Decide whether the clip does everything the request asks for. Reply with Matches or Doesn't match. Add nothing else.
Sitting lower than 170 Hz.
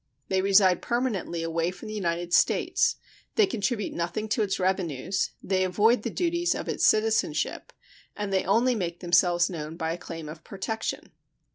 Doesn't match